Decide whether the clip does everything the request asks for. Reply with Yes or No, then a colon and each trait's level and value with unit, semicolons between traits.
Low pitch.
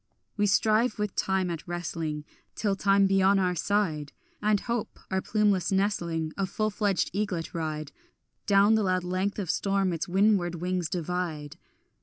No: high, 190 Hz